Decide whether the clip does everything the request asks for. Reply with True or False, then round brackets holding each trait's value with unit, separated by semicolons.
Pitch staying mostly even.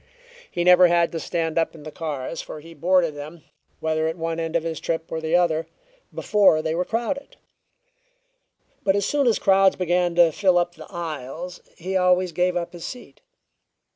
True (2.1 semitones)